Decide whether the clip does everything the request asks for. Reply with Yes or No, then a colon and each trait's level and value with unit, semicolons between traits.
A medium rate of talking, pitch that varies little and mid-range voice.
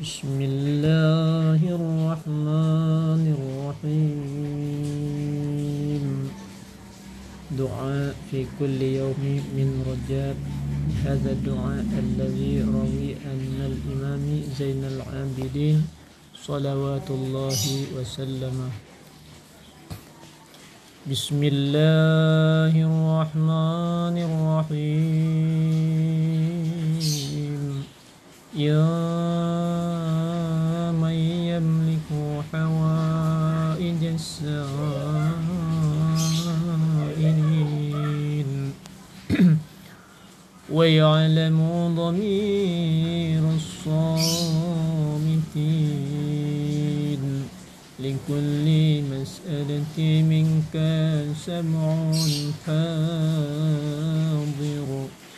No: slow, 40 wpm; narrow, 2.2 semitones; medium, 155 Hz